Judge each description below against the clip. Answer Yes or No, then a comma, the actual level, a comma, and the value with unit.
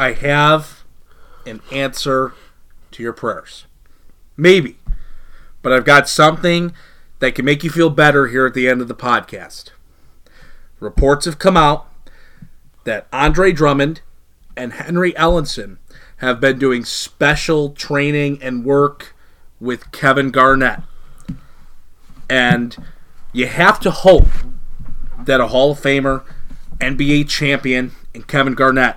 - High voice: No, low, 135 Hz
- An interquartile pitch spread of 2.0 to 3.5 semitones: Yes, average, 2.9 semitones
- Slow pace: Yes, slow, 125 wpm